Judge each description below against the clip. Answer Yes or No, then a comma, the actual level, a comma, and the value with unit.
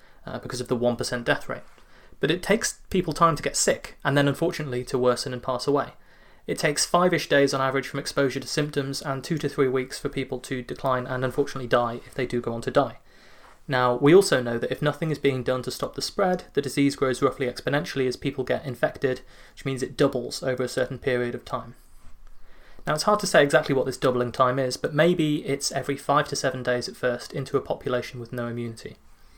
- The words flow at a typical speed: No, fast, 230 wpm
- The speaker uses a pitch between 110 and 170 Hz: Yes, low, 135 Hz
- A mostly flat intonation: Yes, narrow, 2.2 semitones